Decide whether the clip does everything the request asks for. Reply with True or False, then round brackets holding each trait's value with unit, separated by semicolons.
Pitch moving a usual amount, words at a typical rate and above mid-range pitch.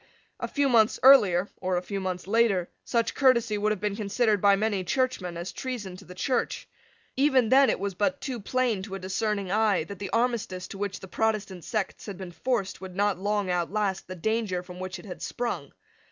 False (3.7 semitones; 210 wpm; 205 Hz)